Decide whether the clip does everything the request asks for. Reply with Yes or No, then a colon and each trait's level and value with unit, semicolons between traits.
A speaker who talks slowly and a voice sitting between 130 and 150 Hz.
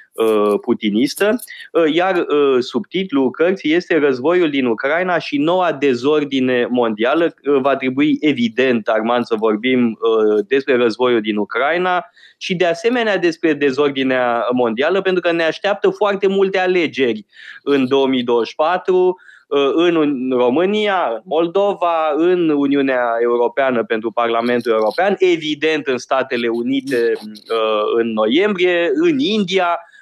Yes: slow, 110 wpm; medium, 140 Hz